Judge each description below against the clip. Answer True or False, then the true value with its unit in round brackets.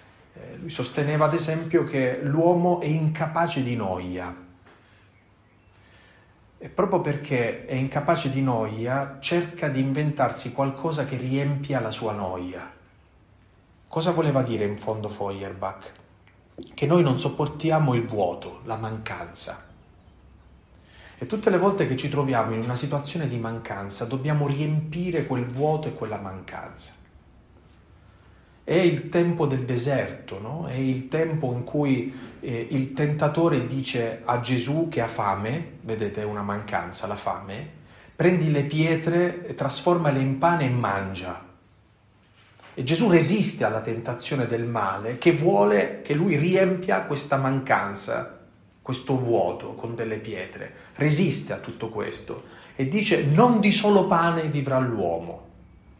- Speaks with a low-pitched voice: True (130 Hz)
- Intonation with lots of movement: True (6.7 semitones)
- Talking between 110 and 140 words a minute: True (135 wpm)